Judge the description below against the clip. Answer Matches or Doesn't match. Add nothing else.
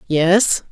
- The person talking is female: Matches